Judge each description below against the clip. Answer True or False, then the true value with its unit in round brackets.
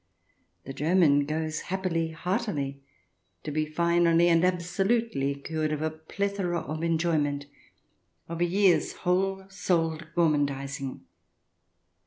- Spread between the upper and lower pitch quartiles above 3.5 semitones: False (2.8 semitones)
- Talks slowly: True (110 wpm)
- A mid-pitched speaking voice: True (165 Hz)